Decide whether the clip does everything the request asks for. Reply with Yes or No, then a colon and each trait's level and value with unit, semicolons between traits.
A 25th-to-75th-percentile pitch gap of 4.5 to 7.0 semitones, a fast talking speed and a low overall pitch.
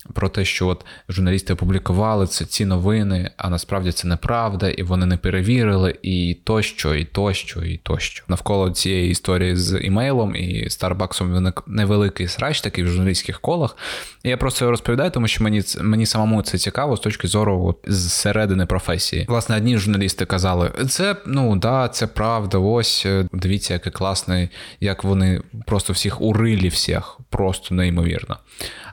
No: average, 3.1 semitones; fast, 160 wpm; very low, 95 Hz